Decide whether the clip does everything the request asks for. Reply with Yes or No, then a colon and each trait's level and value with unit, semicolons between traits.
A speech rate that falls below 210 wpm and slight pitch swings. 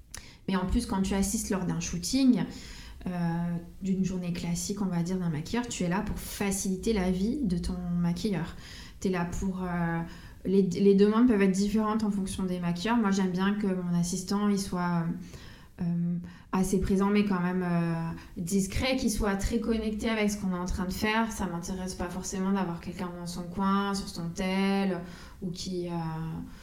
Yes: average, 195 wpm; narrow, 2.2 semitones